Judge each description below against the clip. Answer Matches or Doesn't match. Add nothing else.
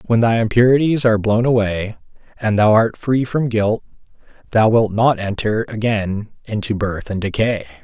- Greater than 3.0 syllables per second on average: Matches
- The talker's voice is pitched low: Matches